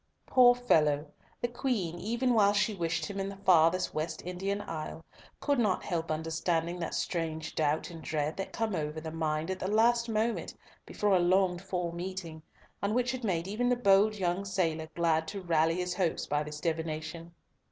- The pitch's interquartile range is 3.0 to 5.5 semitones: Yes, average, 4.0 semitones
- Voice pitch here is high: No, medium, 180 Hz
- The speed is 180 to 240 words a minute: Yes, average, 185 wpm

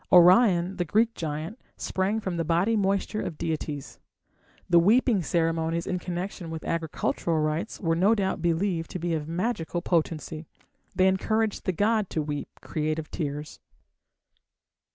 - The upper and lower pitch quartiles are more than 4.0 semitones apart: No, average, 3.4 semitones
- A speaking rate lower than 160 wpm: Yes, average, 145 wpm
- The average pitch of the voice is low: No, medium, 175 Hz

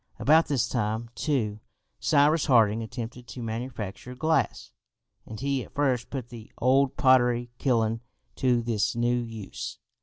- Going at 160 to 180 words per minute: No, average, 140 wpm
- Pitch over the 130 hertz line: No, low, 120 Hz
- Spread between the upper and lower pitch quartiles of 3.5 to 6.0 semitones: No, average, 2.9 semitones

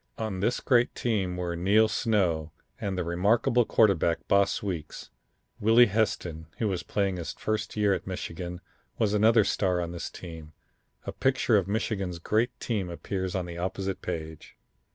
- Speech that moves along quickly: No, average, 160 wpm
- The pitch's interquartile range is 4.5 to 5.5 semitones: No, average, 3.7 semitones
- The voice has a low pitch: Yes, very low, 95 Hz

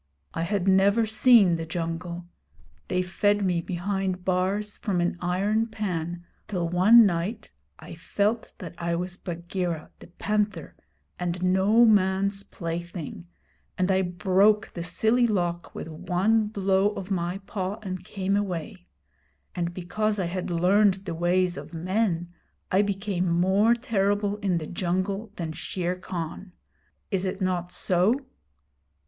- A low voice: No, medium, 185 Hz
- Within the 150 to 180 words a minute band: No, average, 140 wpm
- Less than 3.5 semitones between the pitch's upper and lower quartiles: Yes, average, 2.7 semitones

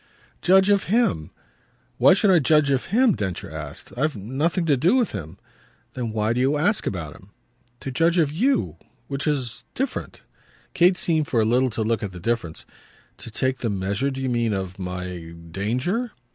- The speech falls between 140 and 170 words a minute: No, average, 185 wpm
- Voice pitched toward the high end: No, low, 130 Hz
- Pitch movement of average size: No, wide, 8.3 semitones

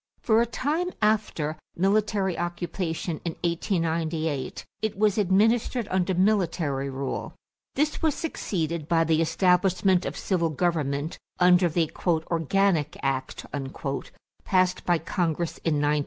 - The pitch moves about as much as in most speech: Yes, average, 3.5 semitones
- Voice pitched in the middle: Yes, medium, 175 Hz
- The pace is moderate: No, slow, 120 wpm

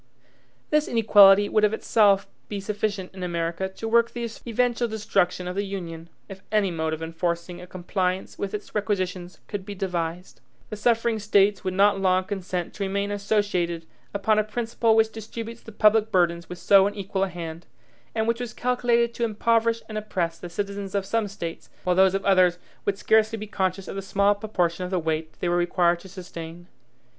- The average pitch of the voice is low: No, high, 195 Hz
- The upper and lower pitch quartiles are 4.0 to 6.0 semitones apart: No, average, 3.2 semitones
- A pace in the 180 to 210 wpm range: Yes, average, 190 wpm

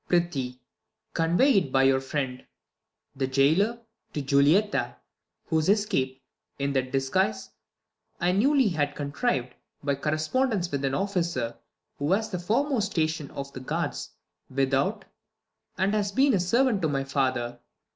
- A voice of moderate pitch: Yes, medium, 155 Hz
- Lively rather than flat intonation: Yes, wide, 6.7 semitones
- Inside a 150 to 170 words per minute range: No, slow, 135 wpm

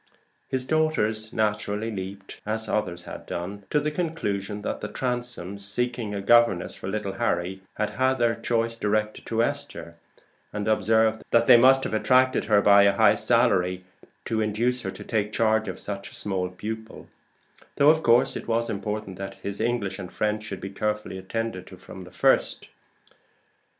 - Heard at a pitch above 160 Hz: No, low, 110 Hz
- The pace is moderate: Yes, average, 175 wpm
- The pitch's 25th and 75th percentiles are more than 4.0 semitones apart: No, average, 2.9 semitones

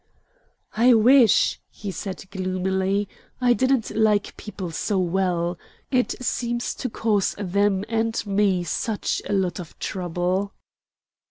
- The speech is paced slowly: Yes, slow, 120 wpm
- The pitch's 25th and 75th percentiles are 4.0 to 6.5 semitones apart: No, average, 3.2 semitones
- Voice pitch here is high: Yes, high, 200 Hz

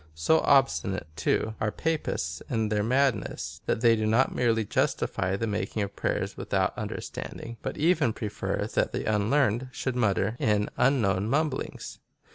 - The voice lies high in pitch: No, low, 110 Hz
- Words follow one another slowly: No, average, 155 wpm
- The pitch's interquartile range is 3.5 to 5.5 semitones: Yes, average, 4.2 semitones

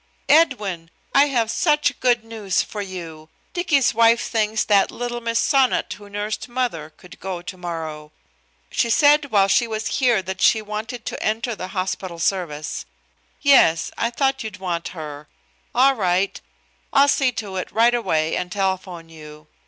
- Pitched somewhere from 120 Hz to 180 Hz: No, high, 210 Hz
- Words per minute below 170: Yes, average, 160 wpm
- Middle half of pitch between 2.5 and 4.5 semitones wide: No, average, 5.2 semitones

